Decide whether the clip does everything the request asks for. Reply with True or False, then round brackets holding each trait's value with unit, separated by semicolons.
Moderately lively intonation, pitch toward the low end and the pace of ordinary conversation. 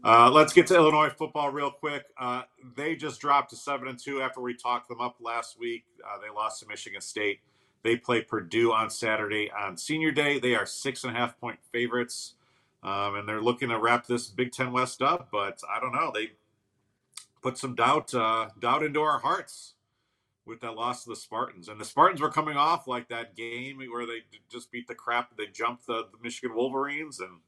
False (3.3 semitones; 120 Hz; 210 wpm)